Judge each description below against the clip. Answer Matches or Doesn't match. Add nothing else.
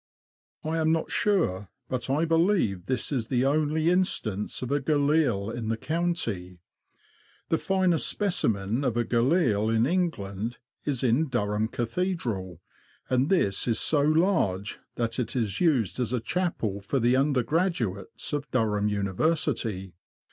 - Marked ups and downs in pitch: Matches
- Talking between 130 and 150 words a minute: Matches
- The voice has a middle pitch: Doesn't match